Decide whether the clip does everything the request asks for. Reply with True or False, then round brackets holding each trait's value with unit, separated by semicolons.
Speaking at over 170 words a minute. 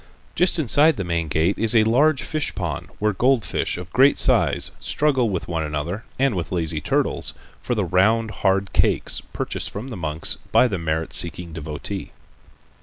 True (180 wpm)